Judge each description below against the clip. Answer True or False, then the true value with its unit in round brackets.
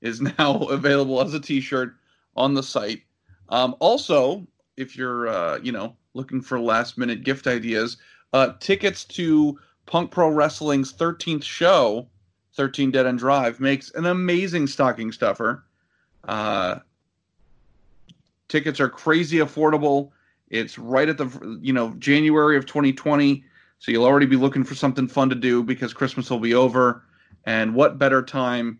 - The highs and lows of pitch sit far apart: False (3.2 semitones)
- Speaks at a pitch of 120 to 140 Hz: True (135 Hz)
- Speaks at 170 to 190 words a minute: False (150 wpm)